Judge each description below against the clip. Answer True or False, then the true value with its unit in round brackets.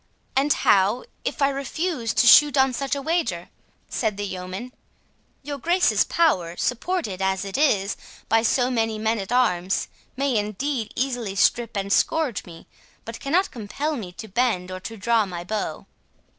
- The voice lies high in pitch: True (230 Hz)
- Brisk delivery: False (160 wpm)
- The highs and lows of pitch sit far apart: True (5.9 semitones)